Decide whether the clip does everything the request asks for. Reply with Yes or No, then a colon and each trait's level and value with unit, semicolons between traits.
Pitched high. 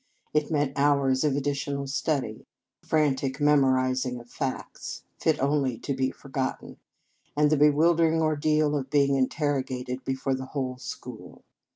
No: medium, 140 Hz